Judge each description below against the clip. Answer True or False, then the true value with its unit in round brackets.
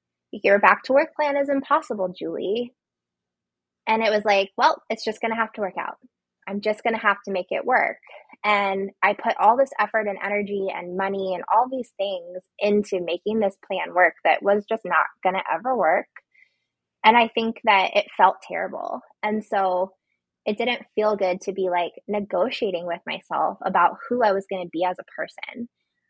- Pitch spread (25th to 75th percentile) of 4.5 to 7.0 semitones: False (3.5 semitones)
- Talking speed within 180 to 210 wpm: True (200 wpm)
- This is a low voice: False (205 Hz)